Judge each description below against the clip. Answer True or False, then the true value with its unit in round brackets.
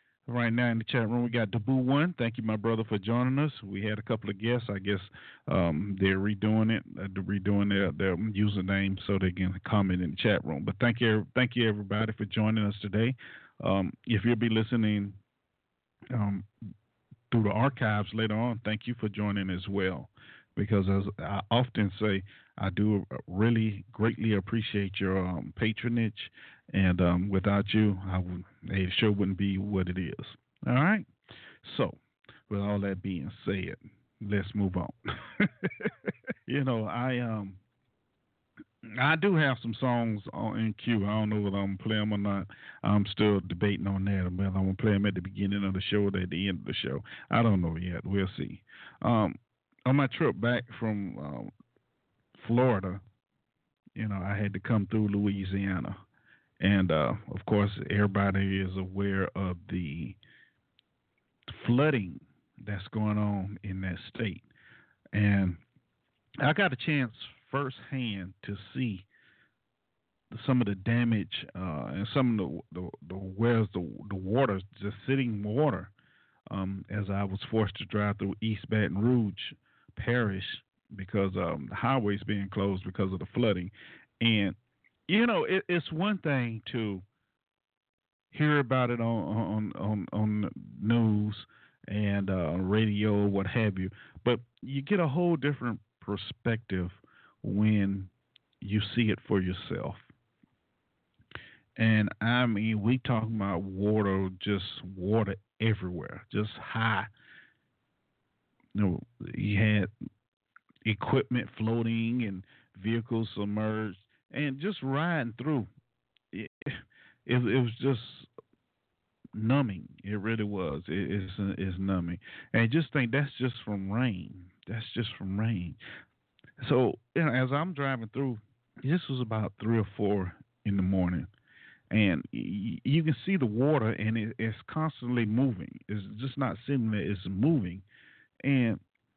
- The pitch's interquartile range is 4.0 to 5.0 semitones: False (3.2 semitones)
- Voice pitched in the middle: False (105 Hz)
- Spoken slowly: False (155 wpm)